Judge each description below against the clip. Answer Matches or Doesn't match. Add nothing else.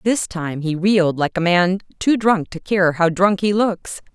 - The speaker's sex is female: Matches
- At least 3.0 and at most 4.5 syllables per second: Matches